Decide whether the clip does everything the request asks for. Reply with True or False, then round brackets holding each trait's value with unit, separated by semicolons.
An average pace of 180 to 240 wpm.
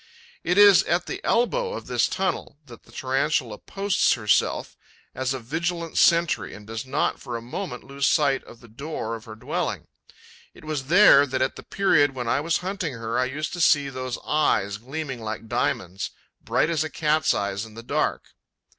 True (190 wpm)